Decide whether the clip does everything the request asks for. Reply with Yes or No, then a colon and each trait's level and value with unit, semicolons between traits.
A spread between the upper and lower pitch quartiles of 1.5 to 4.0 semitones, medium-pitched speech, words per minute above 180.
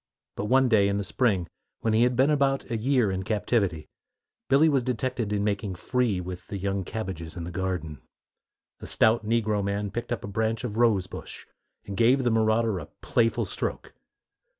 No: average, 3.6 semitones; low, 110 Hz; average, 190 wpm